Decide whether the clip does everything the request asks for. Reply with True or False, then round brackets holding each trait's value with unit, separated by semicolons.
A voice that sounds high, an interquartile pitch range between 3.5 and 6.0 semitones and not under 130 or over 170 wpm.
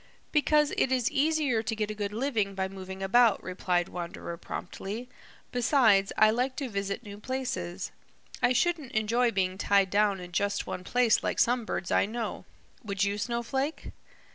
True (215 Hz; 4.2 semitones; 165 wpm)